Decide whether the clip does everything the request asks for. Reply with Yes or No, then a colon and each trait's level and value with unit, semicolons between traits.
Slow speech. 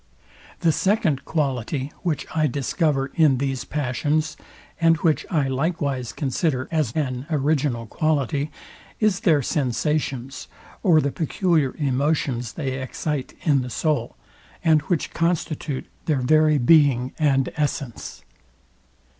Yes: slow, 120 wpm